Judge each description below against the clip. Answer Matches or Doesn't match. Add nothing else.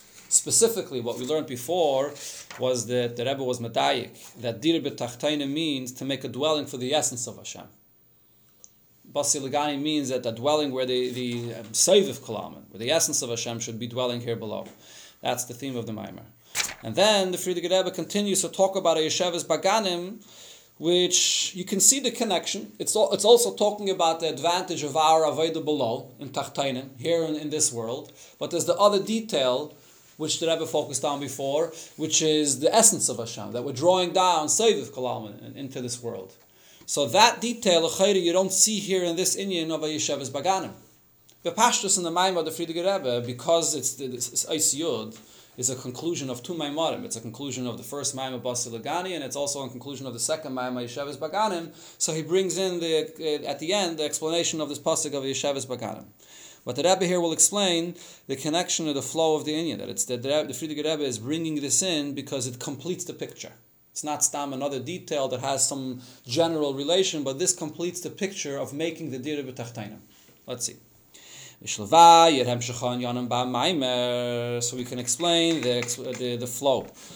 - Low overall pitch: Doesn't match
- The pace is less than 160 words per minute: Doesn't match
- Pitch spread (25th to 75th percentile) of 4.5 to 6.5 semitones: Matches